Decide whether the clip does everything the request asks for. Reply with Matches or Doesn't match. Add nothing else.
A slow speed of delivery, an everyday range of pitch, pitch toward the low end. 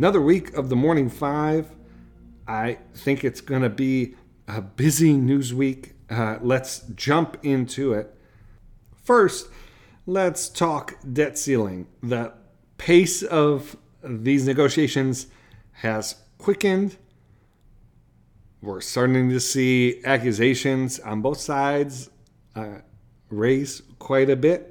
Matches